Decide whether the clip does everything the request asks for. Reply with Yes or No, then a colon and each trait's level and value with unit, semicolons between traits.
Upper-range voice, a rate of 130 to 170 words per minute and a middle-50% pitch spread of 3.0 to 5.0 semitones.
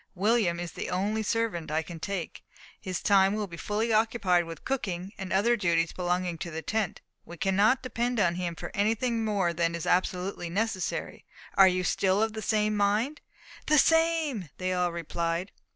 No: high, 195 Hz; average, 180 wpm; average, 4.0 semitones